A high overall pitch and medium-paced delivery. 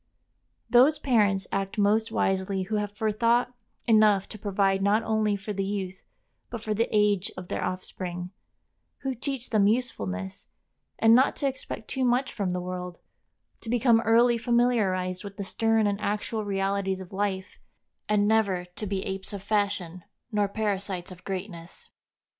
Yes: high, 205 Hz; average, 160 wpm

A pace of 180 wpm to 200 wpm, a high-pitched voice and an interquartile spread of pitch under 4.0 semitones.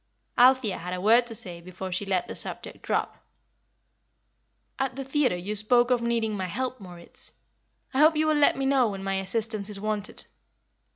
No: average, 185 wpm; high, 215 Hz; average, 5.0 semitones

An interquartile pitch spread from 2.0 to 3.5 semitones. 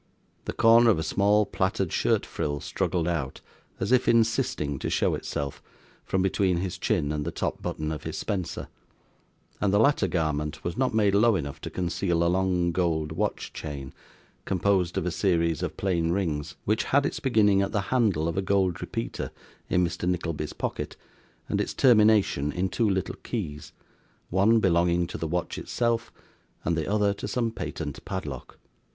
No: average, 4.0 semitones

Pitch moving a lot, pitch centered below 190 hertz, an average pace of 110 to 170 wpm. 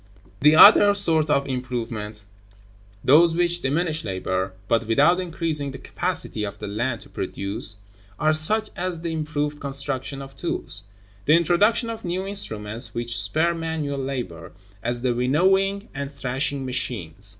Yes: wide, 6.2 semitones; medium, 140 Hz; average, 150 wpm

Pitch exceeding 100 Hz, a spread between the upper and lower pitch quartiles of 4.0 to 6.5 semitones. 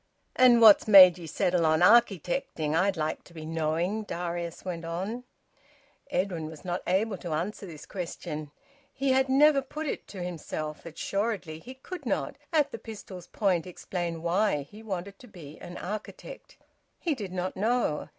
Yes: medium, 185 Hz; average, 4.8 semitones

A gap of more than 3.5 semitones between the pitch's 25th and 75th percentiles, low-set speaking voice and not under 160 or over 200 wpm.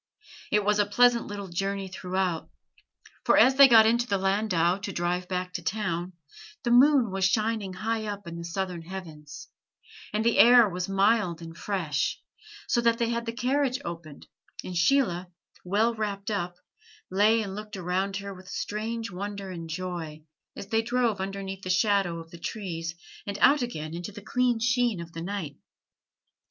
No: average, 3.9 semitones; high, 195 Hz; average, 175 wpm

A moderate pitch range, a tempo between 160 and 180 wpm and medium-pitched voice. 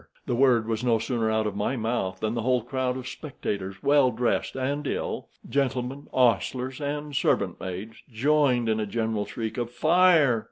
No: average, 3.4 semitones; average, 165 wpm; low, 120 Hz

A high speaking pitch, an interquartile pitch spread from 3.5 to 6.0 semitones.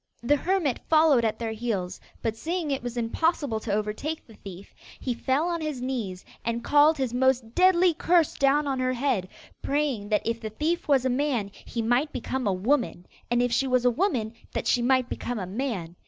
Yes: very high, 250 Hz; average, 4.6 semitones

